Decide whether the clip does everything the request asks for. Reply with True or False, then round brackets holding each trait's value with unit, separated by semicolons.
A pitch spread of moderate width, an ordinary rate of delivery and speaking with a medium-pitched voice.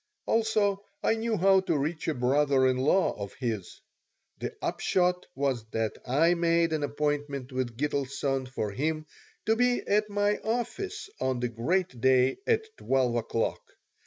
False (7.0 semitones; 155 wpm; 145 Hz)